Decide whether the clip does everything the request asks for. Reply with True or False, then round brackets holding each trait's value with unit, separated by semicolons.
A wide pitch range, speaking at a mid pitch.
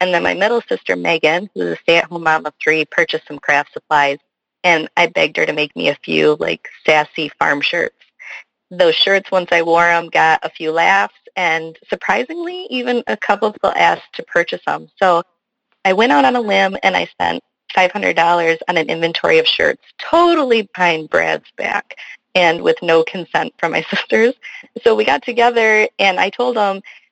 True (7.1 semitones; 180 Hz)